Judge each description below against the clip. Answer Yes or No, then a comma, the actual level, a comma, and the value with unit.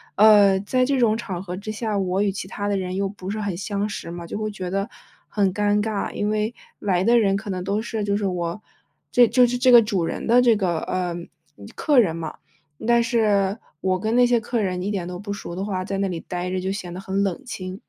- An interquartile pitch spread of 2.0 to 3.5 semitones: Yes, average, 2.7 semitones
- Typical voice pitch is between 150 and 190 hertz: No, high, 200 Hz